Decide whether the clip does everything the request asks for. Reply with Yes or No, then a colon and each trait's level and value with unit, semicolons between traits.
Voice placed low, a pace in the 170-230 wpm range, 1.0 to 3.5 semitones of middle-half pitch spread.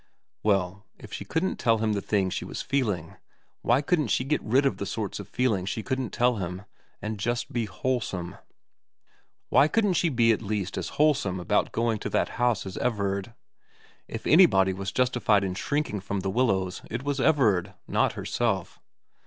No: low, 110 Hz; average, 180 wpm; average, 4.8 semitones